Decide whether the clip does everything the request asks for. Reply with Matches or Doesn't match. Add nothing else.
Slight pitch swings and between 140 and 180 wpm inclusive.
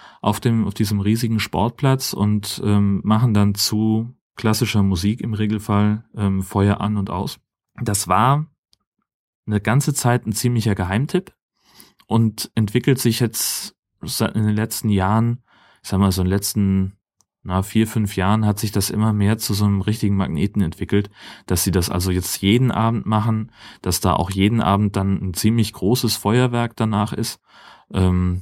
Matches